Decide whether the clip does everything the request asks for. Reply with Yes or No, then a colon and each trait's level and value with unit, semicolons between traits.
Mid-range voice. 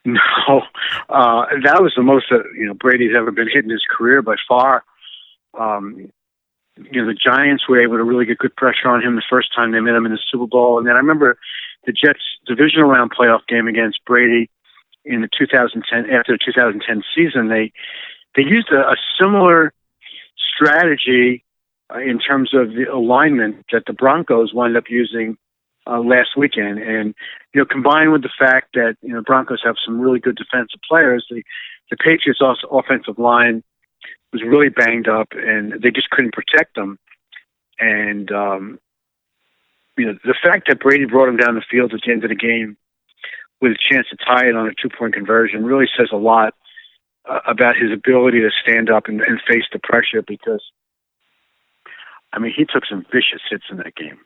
No: low, 120 Hz